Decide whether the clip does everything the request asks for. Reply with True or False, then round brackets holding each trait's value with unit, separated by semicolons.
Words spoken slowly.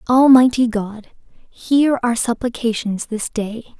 True (110 wpm)